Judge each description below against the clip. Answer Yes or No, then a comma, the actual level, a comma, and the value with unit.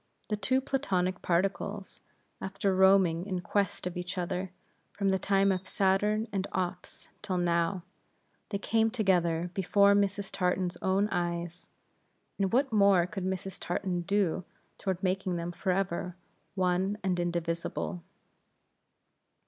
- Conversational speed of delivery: No, slow, 130 wpm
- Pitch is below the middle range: No, high, 190 Hz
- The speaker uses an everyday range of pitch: No, narrow, 2.0 semitones